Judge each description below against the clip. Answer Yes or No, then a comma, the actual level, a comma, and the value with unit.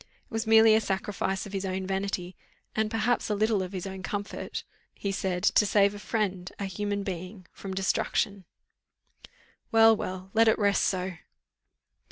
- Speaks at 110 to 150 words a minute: No, average, 170 wpm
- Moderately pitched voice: No, high, 200 Hz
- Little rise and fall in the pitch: Yes, narrow, 2.1 semitones